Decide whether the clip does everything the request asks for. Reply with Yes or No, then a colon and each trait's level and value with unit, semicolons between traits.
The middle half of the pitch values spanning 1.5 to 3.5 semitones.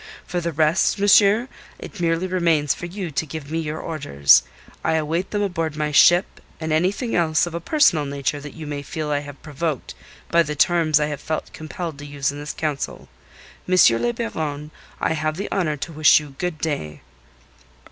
Yes: average, 2.8 semitones